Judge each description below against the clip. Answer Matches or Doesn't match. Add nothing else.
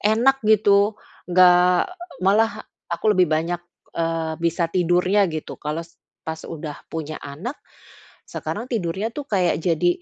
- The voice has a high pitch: Doesn't match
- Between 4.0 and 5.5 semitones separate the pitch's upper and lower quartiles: Matches